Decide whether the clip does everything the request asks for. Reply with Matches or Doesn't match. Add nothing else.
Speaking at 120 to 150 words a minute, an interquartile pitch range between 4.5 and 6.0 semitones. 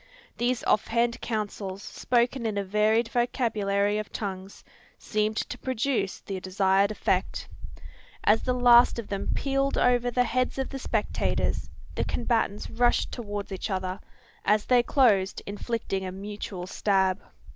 Doesn't match